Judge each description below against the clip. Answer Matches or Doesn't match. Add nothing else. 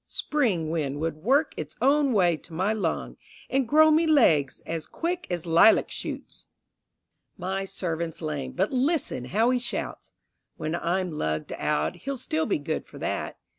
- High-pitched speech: Doesn't match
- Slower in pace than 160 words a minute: Doesn't match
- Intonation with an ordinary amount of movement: Doesn't match